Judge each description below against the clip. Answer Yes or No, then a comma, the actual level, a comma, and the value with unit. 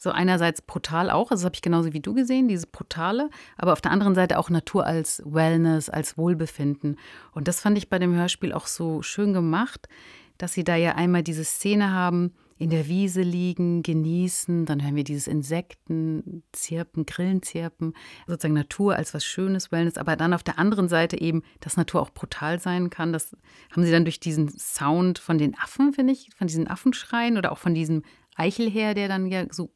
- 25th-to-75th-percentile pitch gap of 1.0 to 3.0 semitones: Yes, narrow, 2.4 semitones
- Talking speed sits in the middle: No, fast, 205 wpm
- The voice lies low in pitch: No, medium, 170 Hz